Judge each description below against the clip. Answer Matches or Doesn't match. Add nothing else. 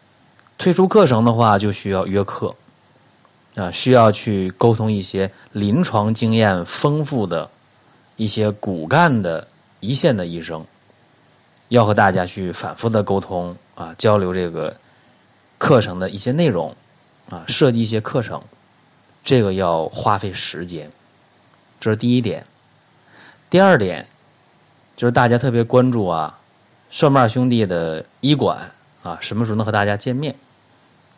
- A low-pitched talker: Matches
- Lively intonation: Doesn't match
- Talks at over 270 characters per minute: Doesn't match